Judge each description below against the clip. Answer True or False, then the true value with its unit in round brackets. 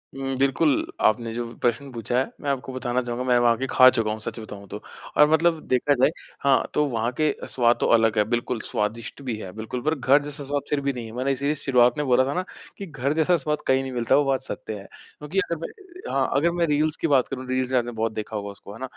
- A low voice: True (130 Hz)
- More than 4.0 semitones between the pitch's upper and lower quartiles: False (3.5 semitones)